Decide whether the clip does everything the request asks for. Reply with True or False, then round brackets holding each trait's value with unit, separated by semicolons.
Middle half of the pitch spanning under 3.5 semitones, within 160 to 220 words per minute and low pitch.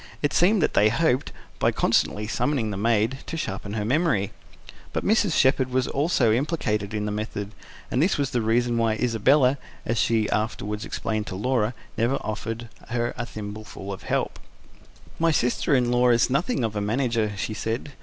False (3.8 semitones; 180 wpm; 115 Hz)